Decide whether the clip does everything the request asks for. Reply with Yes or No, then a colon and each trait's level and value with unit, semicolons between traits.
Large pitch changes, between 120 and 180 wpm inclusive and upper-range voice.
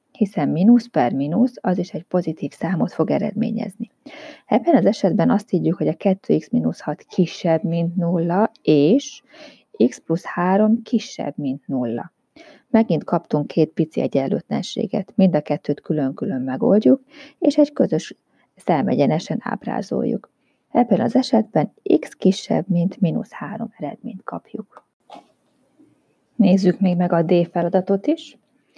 Yes: wide, 6.8 semitones; average, 125 wpm; high, 200 Hz